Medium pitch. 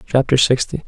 No: low, 130 Hz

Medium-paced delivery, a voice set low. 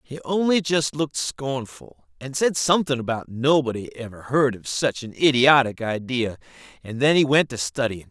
Yes: average, 170 wpm; low, 130 Hz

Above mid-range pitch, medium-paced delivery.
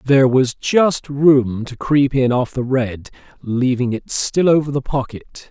No: low, 130 Hz; average, 175 wpm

